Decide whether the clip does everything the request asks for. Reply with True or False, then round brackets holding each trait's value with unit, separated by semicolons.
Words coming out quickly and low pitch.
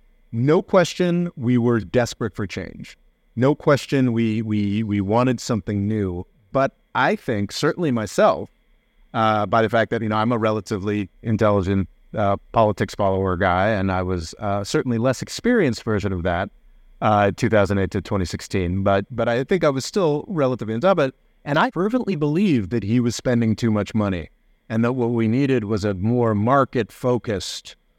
False (175 wpm; 110 Hz)